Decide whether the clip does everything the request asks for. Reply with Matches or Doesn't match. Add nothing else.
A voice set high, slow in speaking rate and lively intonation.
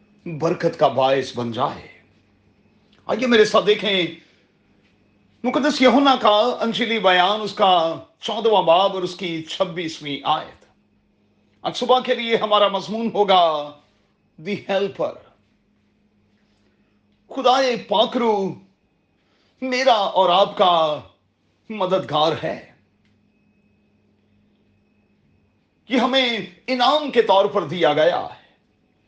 Matches